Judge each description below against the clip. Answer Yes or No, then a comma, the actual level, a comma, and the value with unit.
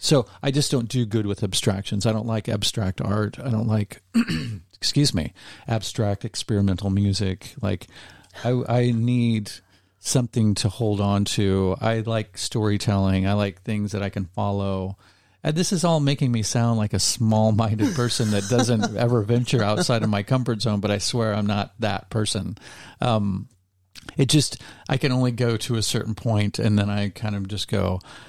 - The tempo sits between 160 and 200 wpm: Yes, average, 180 wpm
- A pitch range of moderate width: Yes, average, 3.1 semitones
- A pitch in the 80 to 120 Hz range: Yes, low, 110 Hz